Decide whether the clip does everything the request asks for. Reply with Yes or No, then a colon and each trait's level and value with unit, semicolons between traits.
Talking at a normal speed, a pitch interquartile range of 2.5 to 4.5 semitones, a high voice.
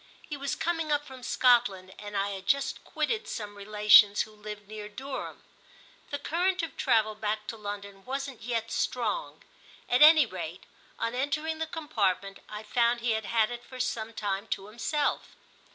No: average, 170 wpm; average, 5.0 semitones; high, 230 Hz